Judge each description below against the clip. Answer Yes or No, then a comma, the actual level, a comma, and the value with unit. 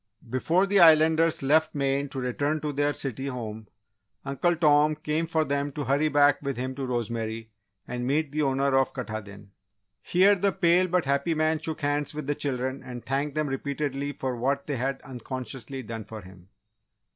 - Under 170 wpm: No, average, 180 wpm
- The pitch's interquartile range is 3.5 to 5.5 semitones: No, average, 3.1 semitones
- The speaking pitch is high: No, medium, 140 Hz